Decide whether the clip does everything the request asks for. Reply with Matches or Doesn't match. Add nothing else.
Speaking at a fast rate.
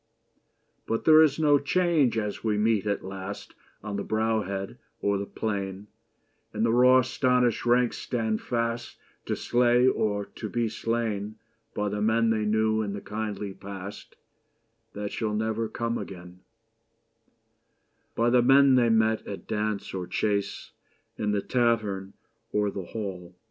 Doesn't match